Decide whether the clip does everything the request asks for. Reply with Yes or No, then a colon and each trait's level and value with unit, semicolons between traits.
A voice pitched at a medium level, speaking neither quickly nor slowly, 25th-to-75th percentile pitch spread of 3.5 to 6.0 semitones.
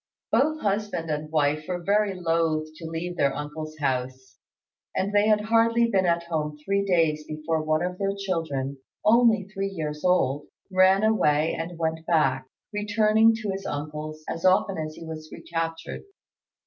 Yes: medium, 165 Hz; average, 165 wpm; average, 4.3 semitones